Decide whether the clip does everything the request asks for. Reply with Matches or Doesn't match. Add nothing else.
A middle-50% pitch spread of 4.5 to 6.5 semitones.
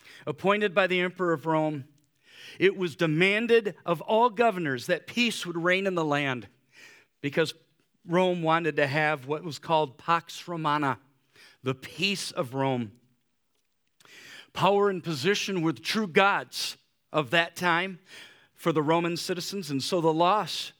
Doesn't match